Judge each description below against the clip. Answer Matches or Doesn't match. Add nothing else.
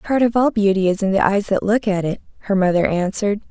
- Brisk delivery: Matches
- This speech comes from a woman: Matches